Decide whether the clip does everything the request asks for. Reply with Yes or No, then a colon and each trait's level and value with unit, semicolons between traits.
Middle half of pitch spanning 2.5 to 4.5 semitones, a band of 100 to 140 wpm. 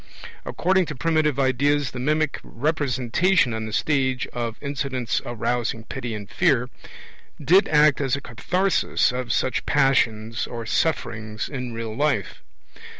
Yes: average, 4.1 semitones; slow, 135 wpm